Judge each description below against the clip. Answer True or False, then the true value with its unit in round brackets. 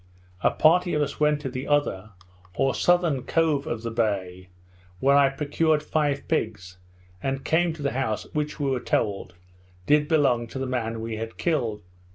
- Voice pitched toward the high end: False (135 Hz)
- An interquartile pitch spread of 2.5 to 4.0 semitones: False (4.9 semitones)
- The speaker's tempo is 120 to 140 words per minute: False (180 wpm)